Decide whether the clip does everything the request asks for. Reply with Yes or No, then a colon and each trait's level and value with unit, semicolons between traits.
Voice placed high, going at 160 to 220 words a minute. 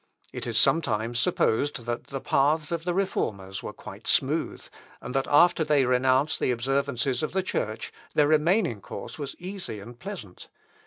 No: low, 135 Hz; average, 165 wpm